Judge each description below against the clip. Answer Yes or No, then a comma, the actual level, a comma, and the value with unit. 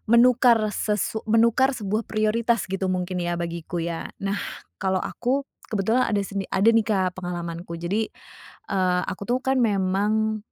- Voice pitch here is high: Yes, high, 200 Hz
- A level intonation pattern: No, average, 3.7 semitones